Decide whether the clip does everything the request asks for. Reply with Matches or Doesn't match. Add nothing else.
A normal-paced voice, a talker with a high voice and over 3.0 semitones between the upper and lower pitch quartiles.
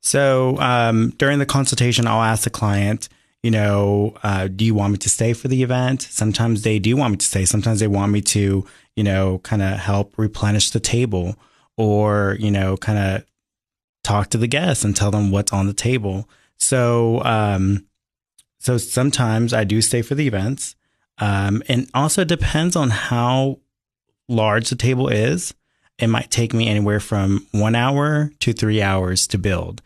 Doesn't match